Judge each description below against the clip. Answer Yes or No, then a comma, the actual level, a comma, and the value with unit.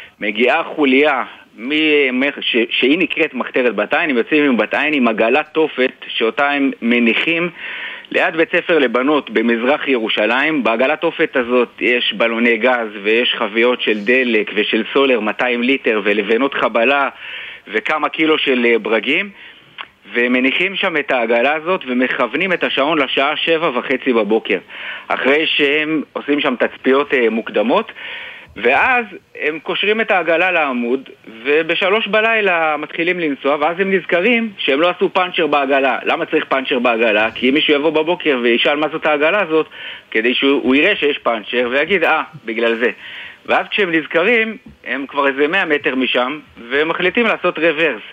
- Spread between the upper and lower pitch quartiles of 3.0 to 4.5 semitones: No, average, 5.1 semitones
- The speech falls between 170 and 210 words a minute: No, average, 145 wpm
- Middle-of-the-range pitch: Yes, medium, 145 Hz